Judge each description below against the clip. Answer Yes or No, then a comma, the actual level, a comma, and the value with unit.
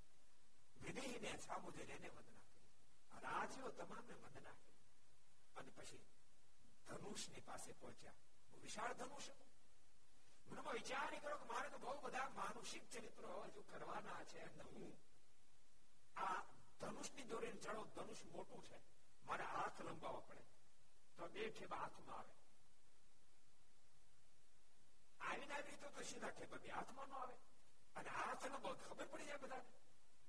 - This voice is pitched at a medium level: No, very high, 260 Hz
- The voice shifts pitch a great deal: No, average, 3.9 semitones